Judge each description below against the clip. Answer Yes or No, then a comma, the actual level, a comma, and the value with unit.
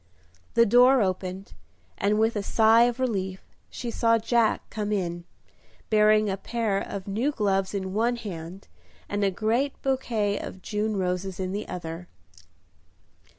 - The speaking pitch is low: No, high, 210 Hz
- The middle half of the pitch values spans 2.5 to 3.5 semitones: Yes, average, 3.2 semitones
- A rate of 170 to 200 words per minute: No, average, 150 wpm